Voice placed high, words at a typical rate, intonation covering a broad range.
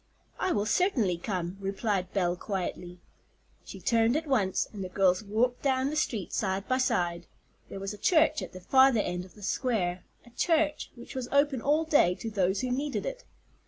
Yes: high, 220 Hz; average, 195 wpm; wide, 6.2 semitones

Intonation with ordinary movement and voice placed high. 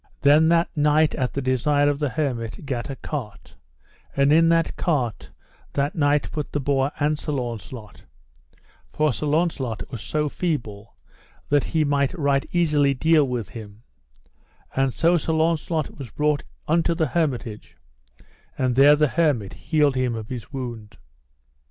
No: average, 3.5 semitones; medium, 145 Hz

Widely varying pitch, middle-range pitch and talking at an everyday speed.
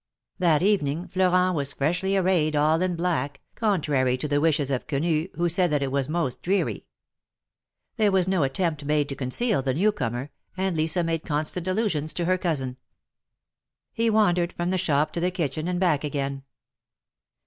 No: average, 4.2 semitones; medium, 165 Hz; average, 175 wpm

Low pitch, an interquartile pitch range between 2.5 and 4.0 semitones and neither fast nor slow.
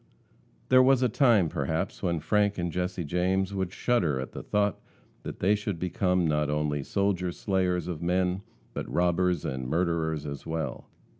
Yes: very low, 90 Hz; average, 3.5 semitones; average, 165 wpm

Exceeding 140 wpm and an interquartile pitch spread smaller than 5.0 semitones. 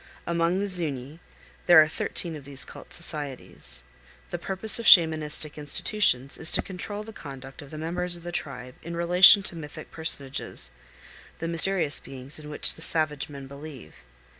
Yes: average, 165 wpm; average, 3.7 semitones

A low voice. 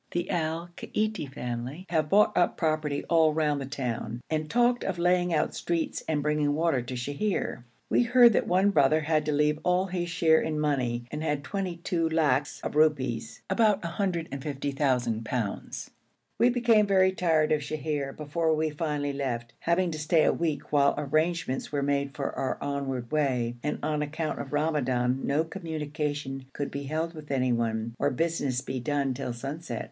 No: medium, 150 Hz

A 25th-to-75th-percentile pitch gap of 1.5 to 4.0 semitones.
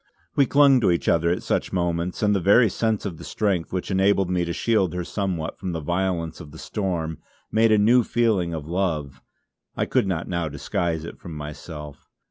Yes: average, 3.6 semitones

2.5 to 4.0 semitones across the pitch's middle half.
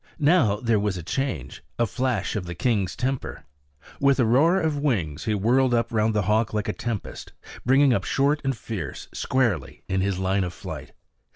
No: wide, 5.4 semitones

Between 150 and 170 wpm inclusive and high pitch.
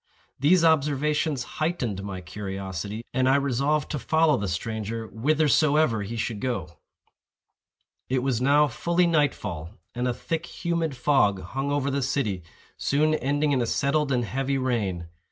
No: average, 155 wpm; low, 130 Hz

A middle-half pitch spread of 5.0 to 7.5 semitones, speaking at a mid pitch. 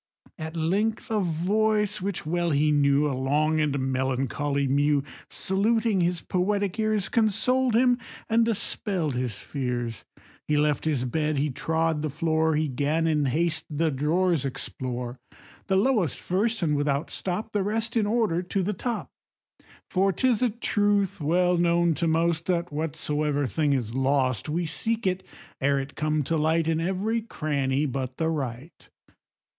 Yes: average, 5.3 semitones; medium, 160 Hz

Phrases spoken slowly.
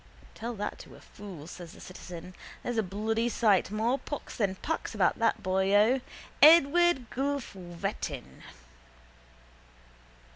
Yes: slow, 125 wpm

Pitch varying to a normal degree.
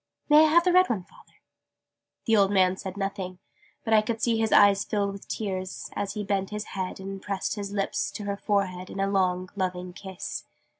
No: narrow, 1.9 semitones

